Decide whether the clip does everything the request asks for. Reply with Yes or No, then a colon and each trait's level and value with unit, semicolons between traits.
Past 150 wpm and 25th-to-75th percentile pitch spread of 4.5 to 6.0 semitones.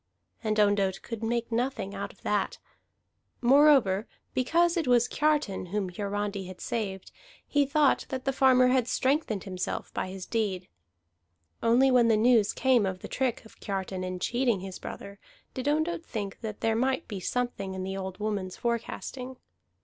Yes: average, 170 wpm; average, 5.0 semitones